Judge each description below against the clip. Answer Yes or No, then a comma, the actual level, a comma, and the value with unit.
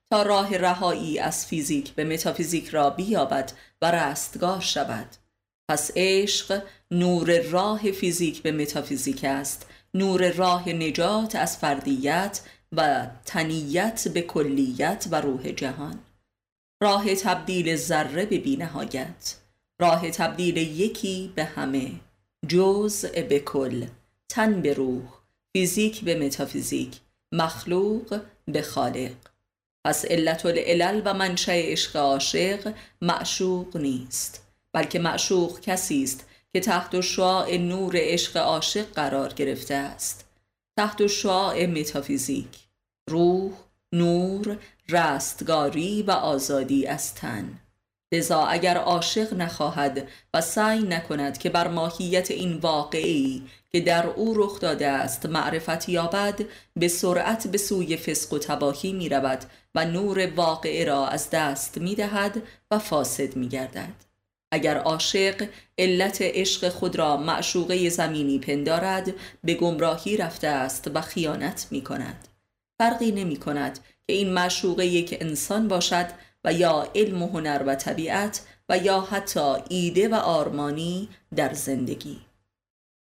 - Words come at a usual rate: Yes, average, 125 wpm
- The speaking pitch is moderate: Yes, medium, 170 Hz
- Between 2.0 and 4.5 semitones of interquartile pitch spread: No, average, 4.9 semitones